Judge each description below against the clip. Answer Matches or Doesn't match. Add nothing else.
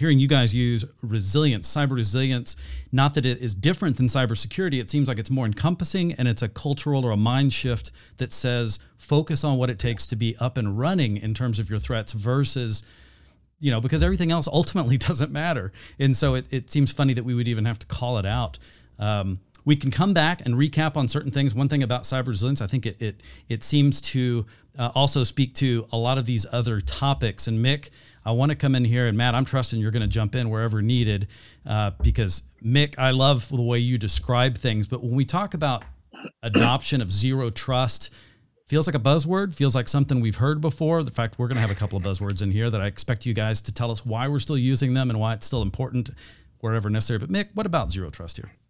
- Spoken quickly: Matches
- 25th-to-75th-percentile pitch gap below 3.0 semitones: Doesn't match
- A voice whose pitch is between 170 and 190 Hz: Doesn't match